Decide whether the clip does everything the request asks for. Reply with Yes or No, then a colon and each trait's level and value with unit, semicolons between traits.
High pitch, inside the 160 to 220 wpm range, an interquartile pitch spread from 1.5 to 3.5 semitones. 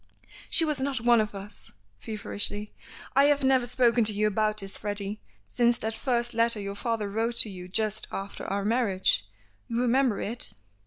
Yes: high, 220 Hz; average, 175 wpm; average, 2.8 semitones